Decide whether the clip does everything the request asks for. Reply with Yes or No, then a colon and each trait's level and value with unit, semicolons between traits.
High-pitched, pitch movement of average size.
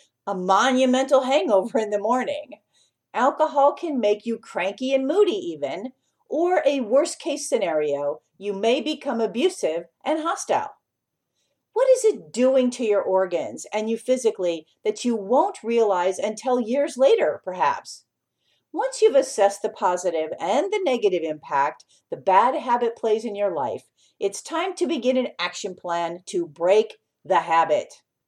No: high, 240 Hz; wide, 6.9 semitones